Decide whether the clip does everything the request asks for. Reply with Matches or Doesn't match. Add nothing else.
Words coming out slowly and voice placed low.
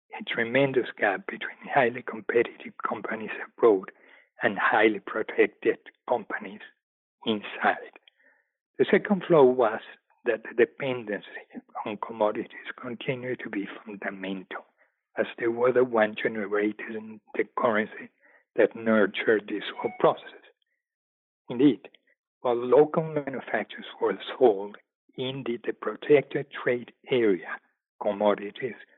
Matches